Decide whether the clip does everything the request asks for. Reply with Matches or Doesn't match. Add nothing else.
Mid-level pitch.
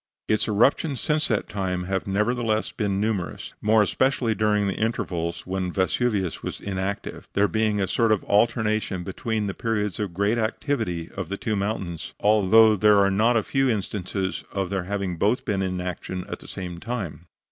Doesn't match